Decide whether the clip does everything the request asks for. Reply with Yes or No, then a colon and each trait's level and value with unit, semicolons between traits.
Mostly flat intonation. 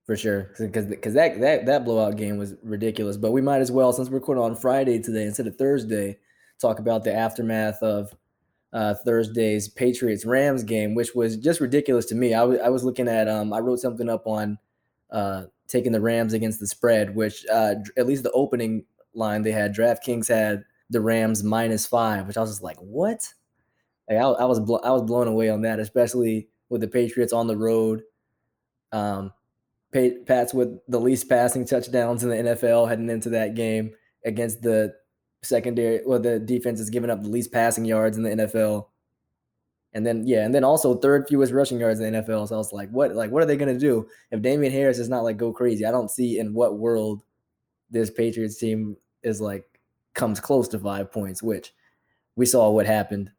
Yes: narrow, 2.1 semitones